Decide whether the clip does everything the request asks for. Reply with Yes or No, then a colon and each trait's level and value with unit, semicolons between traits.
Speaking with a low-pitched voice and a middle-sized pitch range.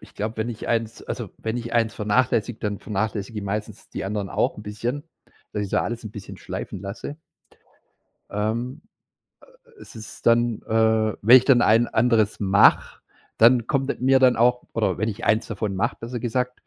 No: low, 110 Hz; narrow, 2.3 semitones